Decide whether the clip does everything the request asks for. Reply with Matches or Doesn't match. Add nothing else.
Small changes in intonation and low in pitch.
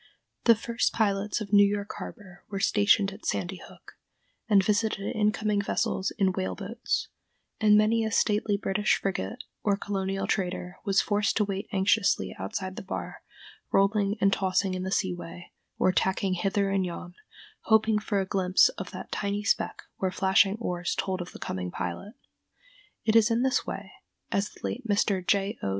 Doesn't match